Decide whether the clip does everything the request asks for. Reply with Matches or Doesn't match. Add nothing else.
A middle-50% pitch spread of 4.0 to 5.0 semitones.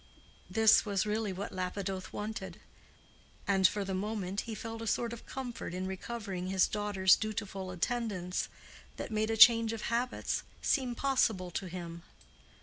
Doesn't match